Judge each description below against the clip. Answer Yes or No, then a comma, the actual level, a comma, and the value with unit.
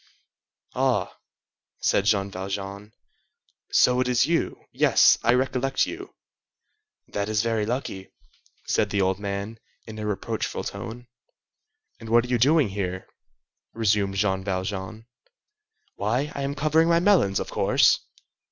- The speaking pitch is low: Yes, low, 110 Hz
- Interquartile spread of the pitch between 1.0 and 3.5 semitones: No, average, 4.2 semitones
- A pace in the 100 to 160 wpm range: Yes, slow, 135 wpm